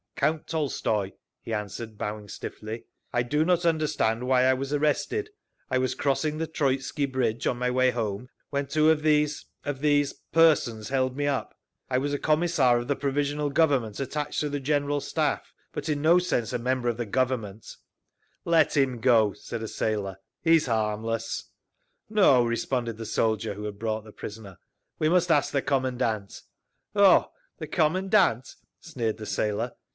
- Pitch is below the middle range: Yes, low, 130 Hz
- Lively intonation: No, average, 4.8 semitones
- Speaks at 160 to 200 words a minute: Yes, average, 165 wpm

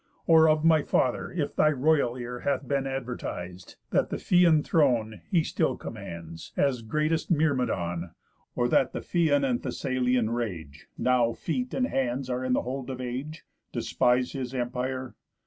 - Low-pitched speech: Yes, low, 130 Hz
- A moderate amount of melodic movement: Yes, average, 3.8 semitones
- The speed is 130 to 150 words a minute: No, average, 160 wpm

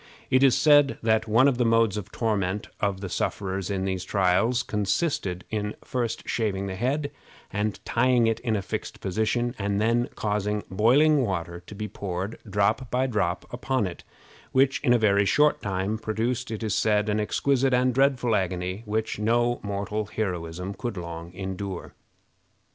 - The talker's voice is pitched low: Yes, low, 105 Hz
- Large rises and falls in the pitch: No, average, 3.7 semitones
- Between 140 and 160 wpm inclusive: No, average, 170 wpm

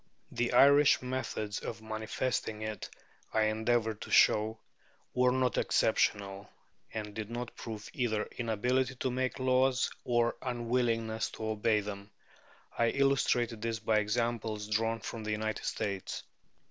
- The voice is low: Yes, low, 115 Hz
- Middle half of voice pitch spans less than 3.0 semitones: Yes, narrow, 2.4 semitones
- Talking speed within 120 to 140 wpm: Yes, slow, 135 wpm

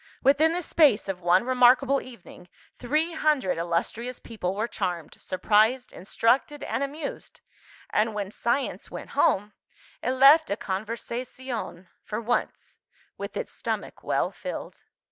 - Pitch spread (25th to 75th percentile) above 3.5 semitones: Yes, average, 5.3 semitones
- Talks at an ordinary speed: No, slow, 130 wpm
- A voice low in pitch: No, high, 235 Hz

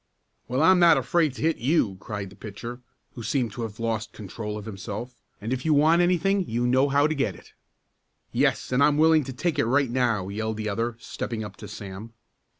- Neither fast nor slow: No, fast, 215 wpm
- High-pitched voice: No, low, 120 Hz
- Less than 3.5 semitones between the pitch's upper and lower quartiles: No, average, 5.2 semitones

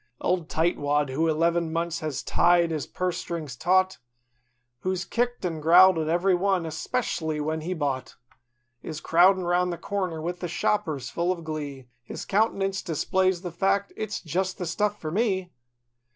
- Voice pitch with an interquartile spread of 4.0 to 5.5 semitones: No, average, 2.9 semitones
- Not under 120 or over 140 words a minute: No, average, 160 wpm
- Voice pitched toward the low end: No, medium, 175 Hz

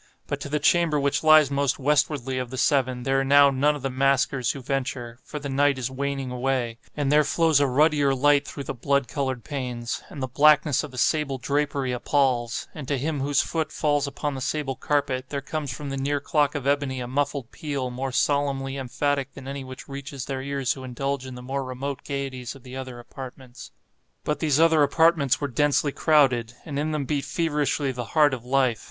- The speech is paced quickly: Yes, fast, 210 wpm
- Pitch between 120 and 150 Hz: Yes, medium, 140 Hz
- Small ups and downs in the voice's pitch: Yes, narrow, 1.9 semitones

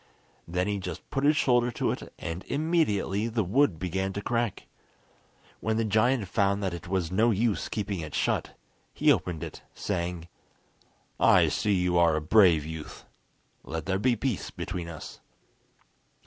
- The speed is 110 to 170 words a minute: Yes, average, 160 wpm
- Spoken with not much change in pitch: No, average, 4.7 semitones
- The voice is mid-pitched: No, very low, 95 Hz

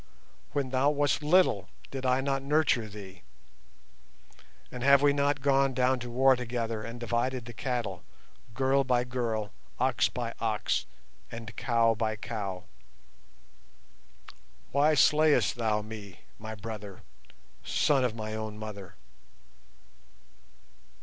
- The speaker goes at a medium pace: No, slow, 125 wpm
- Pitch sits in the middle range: No, low, 120 Hz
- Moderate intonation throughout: Yes, average, 3.6 semitones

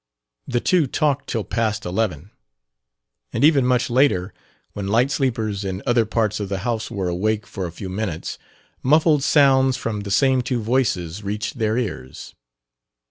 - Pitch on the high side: No, low, 110 Hz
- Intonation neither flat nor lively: Yes, average, 4.6 semitones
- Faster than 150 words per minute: Yes, average, 160 wpm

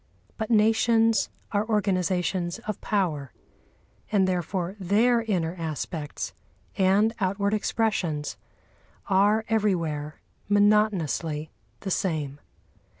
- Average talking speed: No, slow, 90 wpm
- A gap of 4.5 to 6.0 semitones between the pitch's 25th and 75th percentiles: No, average, 4.1 semitones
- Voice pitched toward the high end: Yes, high, 195 Hz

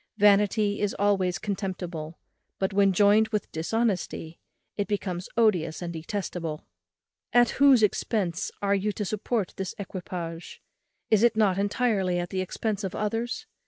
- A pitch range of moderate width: Yes, average, 3.0 semitones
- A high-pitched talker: Yes, high, 200 Hz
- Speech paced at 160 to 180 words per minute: No, average, 140 wpm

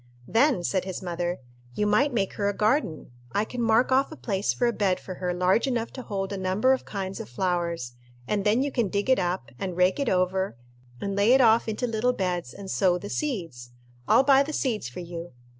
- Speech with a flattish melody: No, average, 4.7 semitones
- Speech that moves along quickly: Yes, fast, 225 wpm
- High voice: Yes, high, 200 Hz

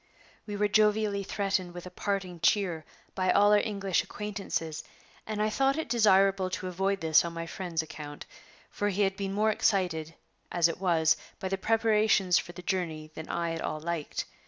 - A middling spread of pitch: Yes, average, 3.4 semitones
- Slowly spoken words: No, average, 185 wpm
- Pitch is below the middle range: No, high, 190 Hz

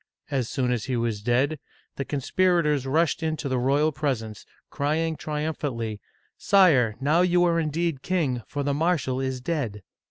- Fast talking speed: No, average, 165 wpm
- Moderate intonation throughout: Yes, average, 4.2 semitones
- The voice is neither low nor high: Yes, medium, 145 Hz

